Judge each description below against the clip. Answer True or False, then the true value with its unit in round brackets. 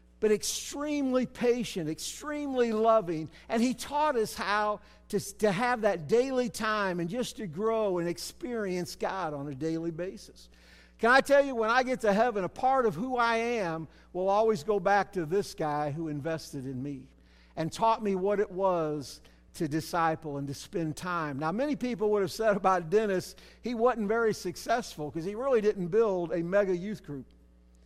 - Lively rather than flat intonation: True (5.8 semitones)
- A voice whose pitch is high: True (200 Hz)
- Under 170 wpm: False (185 wpm)